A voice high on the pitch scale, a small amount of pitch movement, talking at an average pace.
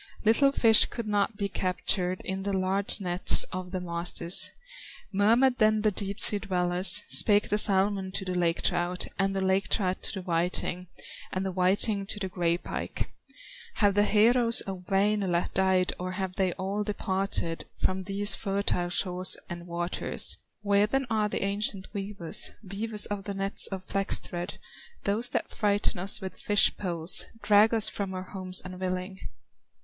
Yes: high, 195 Hz; narrow, 2.0 semitones; average, 165 wpm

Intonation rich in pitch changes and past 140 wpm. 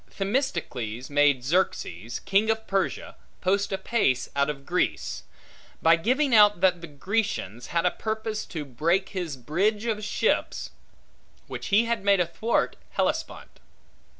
No: wide, 6.5 semitones; slow, 135 wpm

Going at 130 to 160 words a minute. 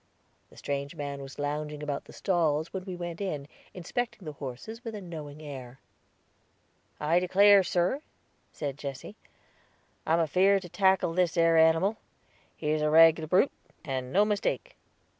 Yes: average, 155 wpm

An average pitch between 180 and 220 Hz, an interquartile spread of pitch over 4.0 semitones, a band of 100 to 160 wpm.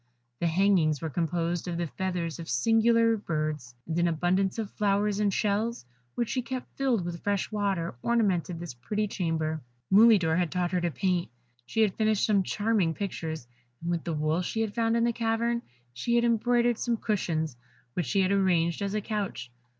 No: high, 190 Hz; average, 4.7 semitones; average, 190 wpm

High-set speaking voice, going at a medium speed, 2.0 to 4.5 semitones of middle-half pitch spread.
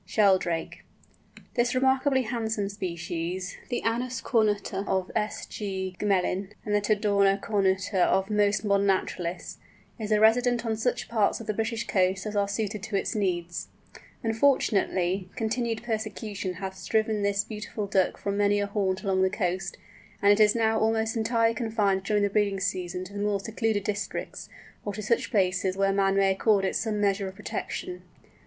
Yes: high, 205 Hz; average, 170 wpm; narrow, 2.4 semitones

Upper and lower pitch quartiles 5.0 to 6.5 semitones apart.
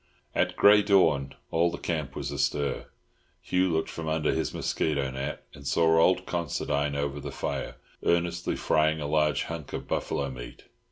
No: average, 3.2 semitones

